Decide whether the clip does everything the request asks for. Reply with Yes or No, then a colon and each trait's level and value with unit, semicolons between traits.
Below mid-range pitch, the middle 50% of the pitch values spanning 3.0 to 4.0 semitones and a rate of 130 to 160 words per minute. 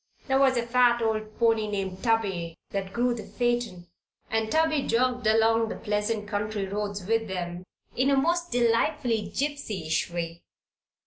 No: high, 225 Hz; average, 3.3 semitones; average, 150 wpm